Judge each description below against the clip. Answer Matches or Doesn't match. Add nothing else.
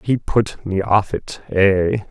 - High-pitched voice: Doesn't match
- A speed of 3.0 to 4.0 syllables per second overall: Matches